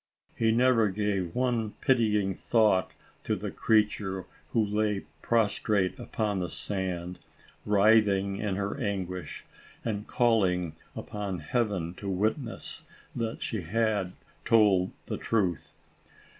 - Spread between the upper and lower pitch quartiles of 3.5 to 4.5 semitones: No, average, 3.0 semitones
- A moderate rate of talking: No, slow, 115 wpm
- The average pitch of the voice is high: No, low, 105 Hz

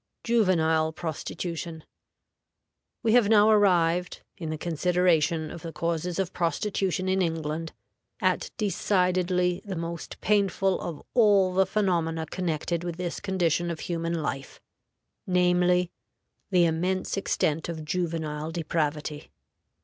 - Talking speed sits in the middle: No, slow, 120 wpm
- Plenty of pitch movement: No, narrow, 2.4 semitones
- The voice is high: No, medium, 175 Hz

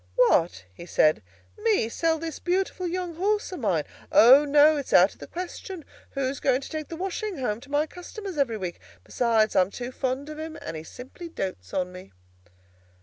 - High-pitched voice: Yes, very high, 280 Hz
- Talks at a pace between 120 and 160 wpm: No, average, 195 wpm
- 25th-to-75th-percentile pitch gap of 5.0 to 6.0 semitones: No, wide, 8.1 semitones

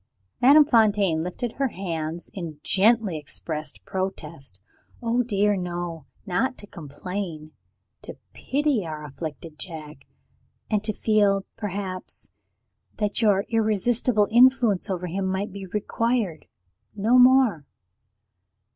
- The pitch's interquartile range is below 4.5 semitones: No, average, 5.0 semitones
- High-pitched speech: Yes, high, 195 Hz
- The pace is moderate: No, slow, 110 wpm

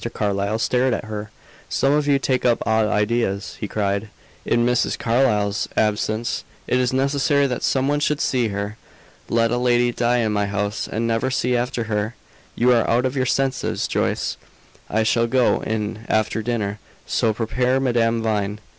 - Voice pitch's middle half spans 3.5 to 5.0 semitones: No, average, 2.8 semitones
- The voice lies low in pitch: Yes, low, 115 Hz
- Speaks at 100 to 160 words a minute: No, average, 175 wpm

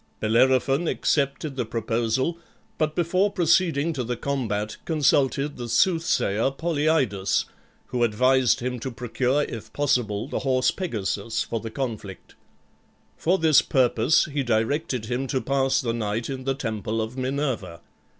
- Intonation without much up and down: No, average, 4.2 semitones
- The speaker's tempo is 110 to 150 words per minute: Yes, average, 140 wpm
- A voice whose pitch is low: Yes, low, 130 Hz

